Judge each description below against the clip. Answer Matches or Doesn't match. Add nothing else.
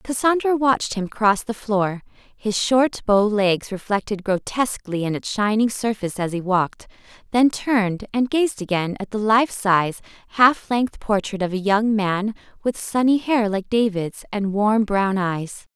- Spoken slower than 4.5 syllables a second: Matches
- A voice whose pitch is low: Doesn't match